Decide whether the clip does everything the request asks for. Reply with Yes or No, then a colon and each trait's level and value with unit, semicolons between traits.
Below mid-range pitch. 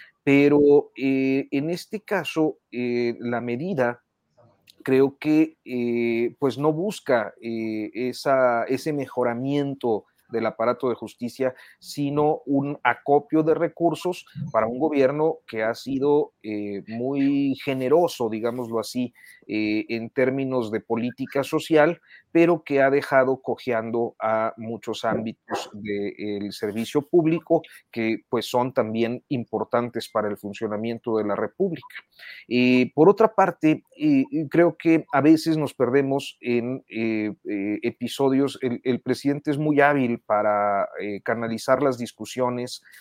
Yes: low, 130 Hz